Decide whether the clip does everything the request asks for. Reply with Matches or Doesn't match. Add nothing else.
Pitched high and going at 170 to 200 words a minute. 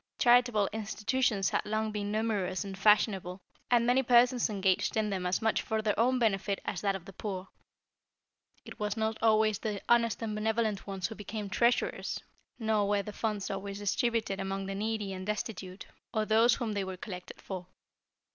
Matches